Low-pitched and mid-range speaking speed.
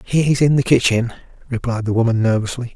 Yes: low, 120 Hz; average, 175 wpm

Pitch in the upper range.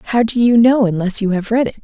Yes: high, 220 Hz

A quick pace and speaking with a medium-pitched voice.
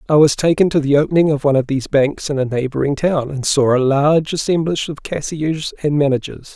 Yes: fast, 220 wpm; medium, 145 Hz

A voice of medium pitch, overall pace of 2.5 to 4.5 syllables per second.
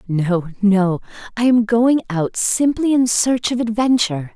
No: high, 220 Hz; 4.1 syllables/s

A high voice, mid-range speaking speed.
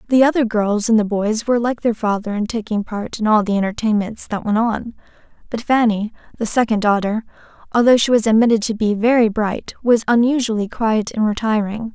Yes: high, 220 Hz; average, 190 wpm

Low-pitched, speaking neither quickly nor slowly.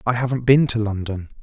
No: low, 115 Hz; fast, 210 wpm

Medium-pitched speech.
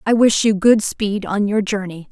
No: high, 205 Hz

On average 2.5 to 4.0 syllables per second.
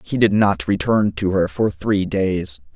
Yes: 3.9 syllables/s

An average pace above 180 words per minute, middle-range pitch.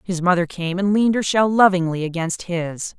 Yes: average, 200 wpm; medium, 180 Hz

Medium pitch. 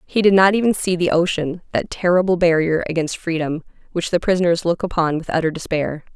Yes: medium, 170 Hz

